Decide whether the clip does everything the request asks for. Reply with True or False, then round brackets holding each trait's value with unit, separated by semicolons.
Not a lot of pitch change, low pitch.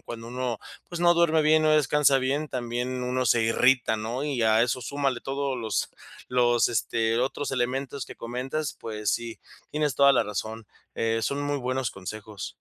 False (3.5 semitones; 125 Hz)